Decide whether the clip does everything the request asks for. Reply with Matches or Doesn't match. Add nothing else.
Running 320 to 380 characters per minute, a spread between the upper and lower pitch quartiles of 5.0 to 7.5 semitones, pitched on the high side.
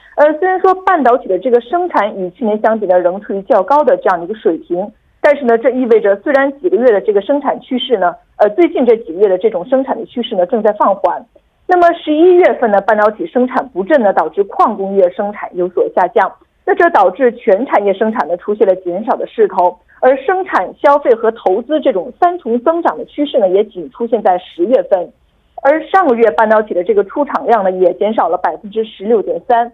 Doesn't match